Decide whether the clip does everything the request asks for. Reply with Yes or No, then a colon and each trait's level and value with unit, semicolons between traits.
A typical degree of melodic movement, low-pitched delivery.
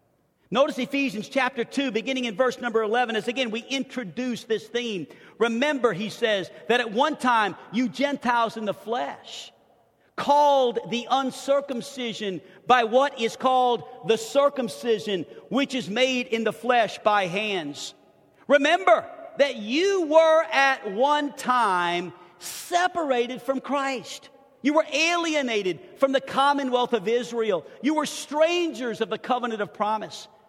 No: average, 3.9 semitones; very high, 250 Hz